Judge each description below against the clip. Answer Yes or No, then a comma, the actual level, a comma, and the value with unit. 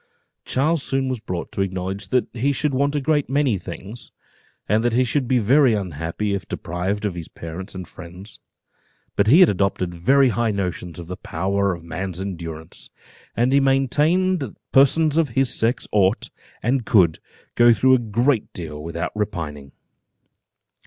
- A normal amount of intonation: No, wide, 6.7 semitones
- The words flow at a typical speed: Yes, average, 170 wpm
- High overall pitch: No, low, 105 Hz